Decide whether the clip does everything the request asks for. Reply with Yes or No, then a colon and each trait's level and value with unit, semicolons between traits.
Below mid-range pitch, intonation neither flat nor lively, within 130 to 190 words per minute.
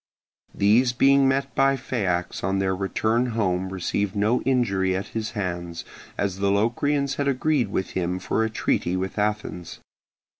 Yes: low, 105 Hz; average, 4.8 semitones; average, 155 wpm